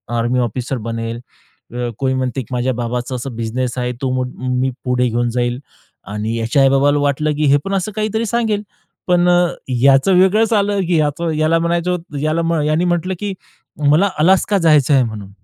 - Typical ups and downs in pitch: No, wide, 6.0 semitones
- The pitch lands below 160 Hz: Yes, medium, 140 Hz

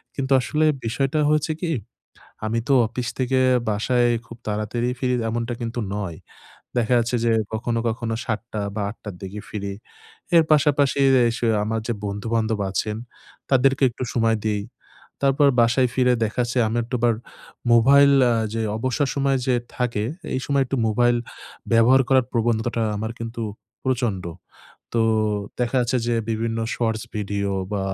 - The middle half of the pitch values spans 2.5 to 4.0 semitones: Yes, average, 2.8 semitones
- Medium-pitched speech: No, low, 120 Hz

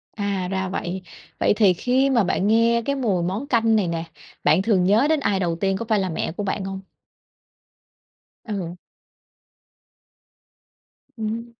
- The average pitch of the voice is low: No, high, 200 Hz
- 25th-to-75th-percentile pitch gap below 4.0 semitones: Yes, average, 3.5 semitones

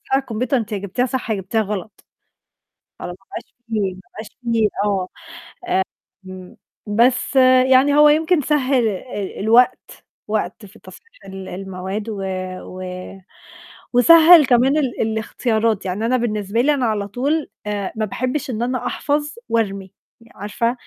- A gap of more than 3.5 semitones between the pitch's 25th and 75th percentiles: Yes, average, 4.2 semitones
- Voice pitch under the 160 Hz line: No, high, 225 Hz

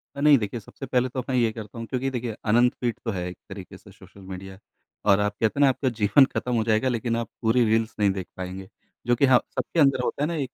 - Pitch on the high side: No, low, 115 Hz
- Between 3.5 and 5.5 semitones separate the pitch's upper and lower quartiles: Yes, average, 3.8 semitones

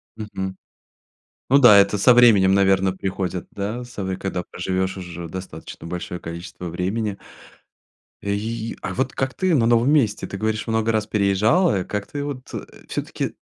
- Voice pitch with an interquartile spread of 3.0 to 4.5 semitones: Yes, average, 3.5 semitones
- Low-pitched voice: Yes, low, 100 Hz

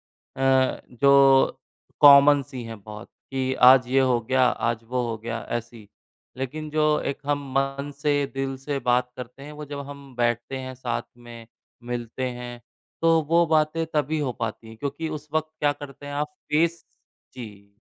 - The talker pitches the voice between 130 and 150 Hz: Yes, low, 135 Hz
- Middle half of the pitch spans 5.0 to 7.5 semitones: No, average, 3.1 semitones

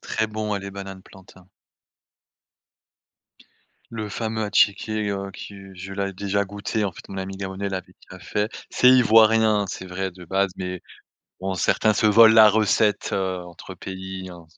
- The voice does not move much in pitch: Yes, narrow, 2.2 semitones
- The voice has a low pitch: Yes, low, 100 Hz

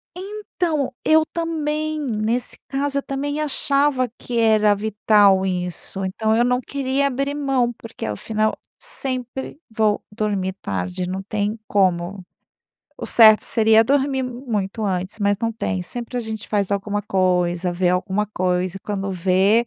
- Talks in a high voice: Yes, high, 220 Hz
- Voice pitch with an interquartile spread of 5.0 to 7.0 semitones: Yes, wide, 5.5 semitones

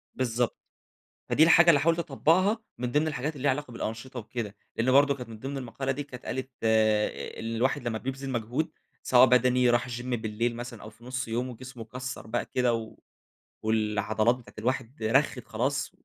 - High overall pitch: No, low, 125 Hz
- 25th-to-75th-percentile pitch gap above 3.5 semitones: No, average, 2.9 semitones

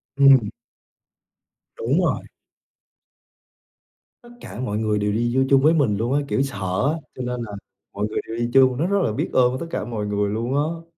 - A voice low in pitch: Yes, low, 125 Hz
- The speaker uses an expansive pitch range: No, average, 4.3 semitones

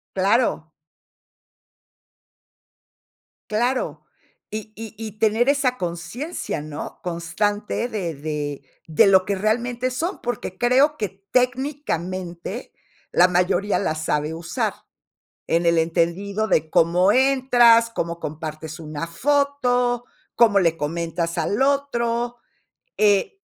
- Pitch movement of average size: No, wide, 6.4 semitones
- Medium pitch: No, high, 200 Hz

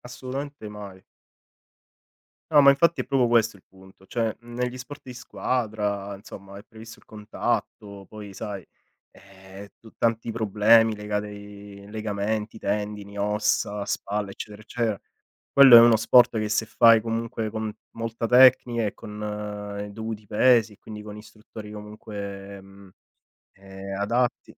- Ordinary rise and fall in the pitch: No, narrow, 2.2 semitones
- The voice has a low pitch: Yes, low, 105 Hz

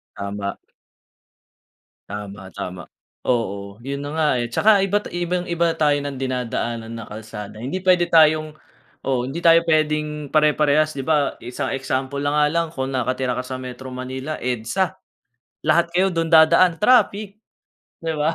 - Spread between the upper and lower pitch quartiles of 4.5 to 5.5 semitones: Yes, average, 4.8 semitones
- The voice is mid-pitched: Yes, medium, 145 Hz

